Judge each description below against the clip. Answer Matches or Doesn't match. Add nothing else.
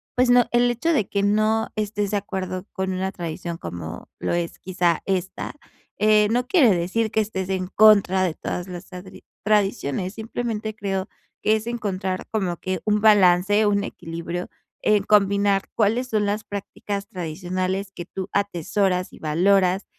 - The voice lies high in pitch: Matches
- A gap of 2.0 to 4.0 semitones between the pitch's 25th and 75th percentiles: Matches